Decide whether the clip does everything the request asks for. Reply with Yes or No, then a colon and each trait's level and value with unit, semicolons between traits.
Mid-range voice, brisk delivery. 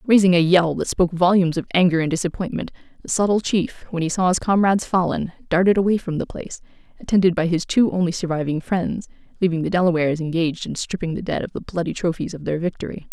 Yes: medium, 175 Hz; fast, 210 wpm